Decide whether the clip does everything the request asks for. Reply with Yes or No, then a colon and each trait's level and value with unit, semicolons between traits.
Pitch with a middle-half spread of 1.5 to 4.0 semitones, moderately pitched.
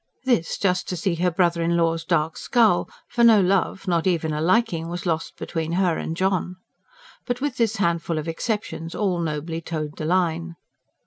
Yes: average, 2.8 semitones; medium, 170 Hz